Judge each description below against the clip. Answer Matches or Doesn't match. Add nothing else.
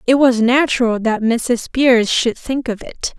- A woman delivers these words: Matches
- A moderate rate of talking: Matches